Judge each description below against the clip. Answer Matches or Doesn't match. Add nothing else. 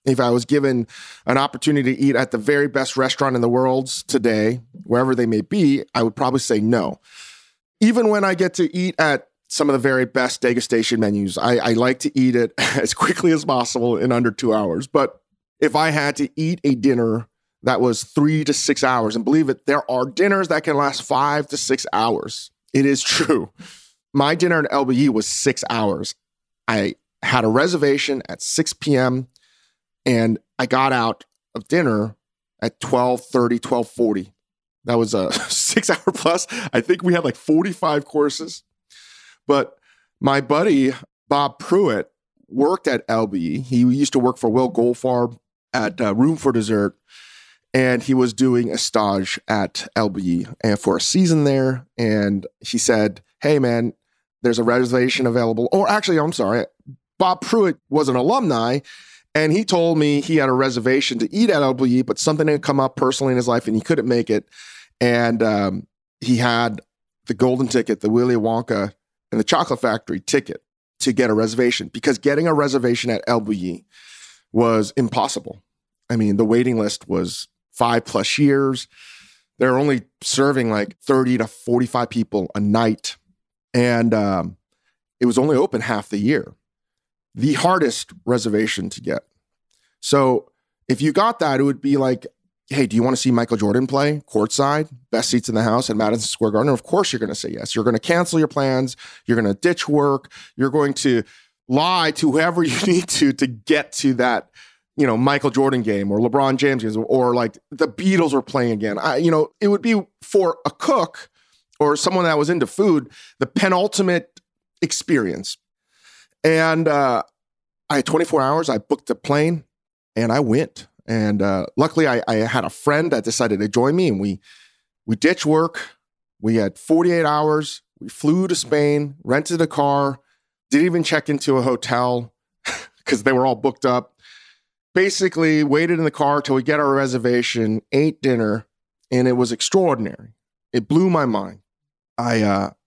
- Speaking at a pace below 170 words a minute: Doesn't match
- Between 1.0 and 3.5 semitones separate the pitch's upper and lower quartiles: Doesn't match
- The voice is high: Doesn't match